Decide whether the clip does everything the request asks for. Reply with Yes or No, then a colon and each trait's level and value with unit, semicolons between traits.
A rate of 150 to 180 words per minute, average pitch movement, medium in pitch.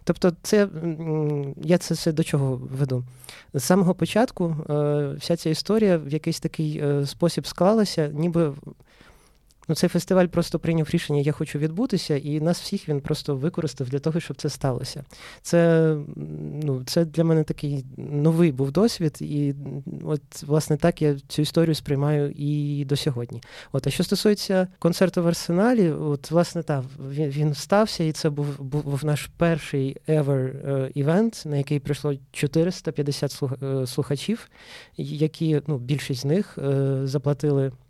Yes: fast, 155 wpm; average, 3.0 semitones; medium, 150 Hz